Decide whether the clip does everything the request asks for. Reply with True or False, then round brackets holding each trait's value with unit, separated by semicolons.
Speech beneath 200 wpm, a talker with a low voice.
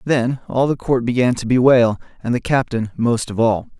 False (205 wpm; 120 Hz)